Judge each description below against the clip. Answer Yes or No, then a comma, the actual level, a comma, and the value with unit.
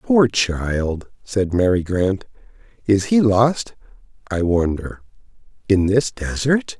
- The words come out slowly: Yes, slow, 115 wpm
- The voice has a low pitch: Yes, low, 100 Hz